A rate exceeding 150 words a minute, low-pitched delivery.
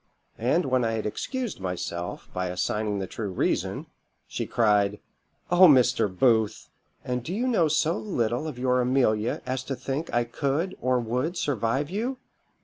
Yes: average, 160 wpm; low, 125 Hz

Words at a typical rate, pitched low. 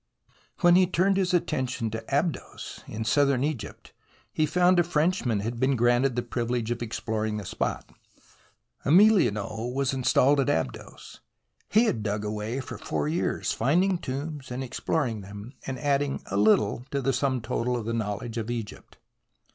Yes: average, 165 wpm; low, 125 Hz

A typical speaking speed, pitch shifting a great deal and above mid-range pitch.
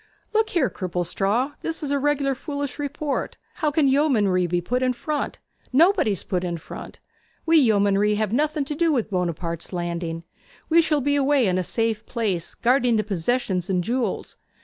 Yes: average, 170 wpm; wide, 7.6 semitones; high, 240 Hz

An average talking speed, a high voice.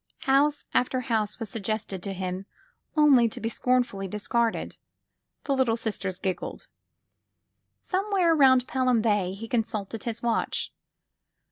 No: slow, 125 wpm; high, 230 Hz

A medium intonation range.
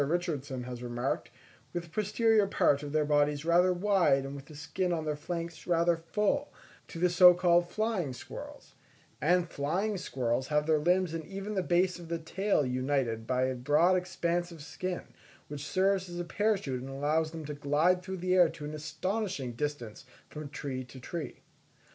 Yes: average, 4.1 semitones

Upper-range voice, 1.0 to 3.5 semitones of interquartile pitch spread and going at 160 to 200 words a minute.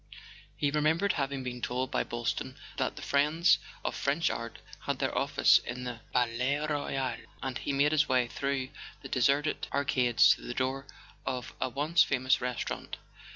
No: low, 135 Hz; narrow, 2.5 semitones; average, 170 wpm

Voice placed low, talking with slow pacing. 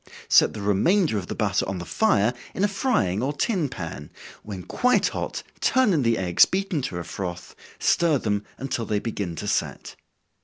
No: low, 115 Hz; average, 190 wpm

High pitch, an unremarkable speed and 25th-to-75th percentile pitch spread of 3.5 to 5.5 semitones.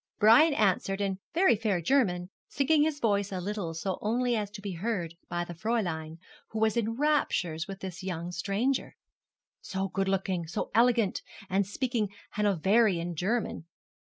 Yes: high, 200 Hz; average, 160 wpm; average, 4.4 semitones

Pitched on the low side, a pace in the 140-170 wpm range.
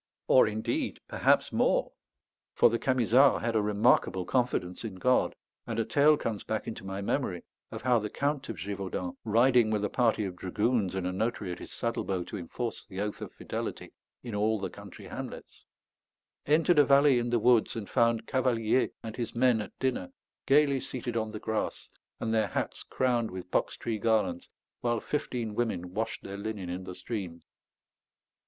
No: low, 110 Hz; average, 180 wpm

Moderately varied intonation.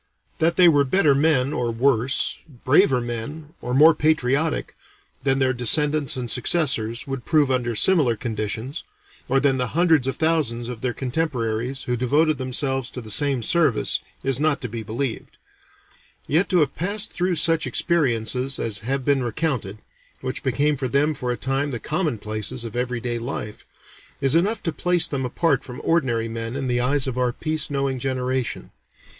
Yes: average, 3.9 semitones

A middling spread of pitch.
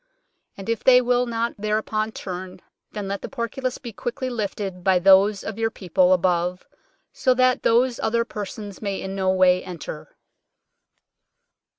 Yes: average, 3.9 semitones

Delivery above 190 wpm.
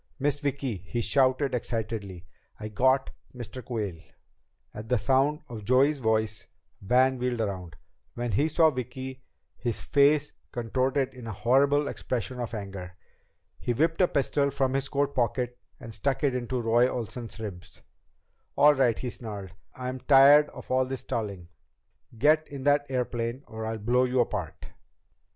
No: average, 155 wpm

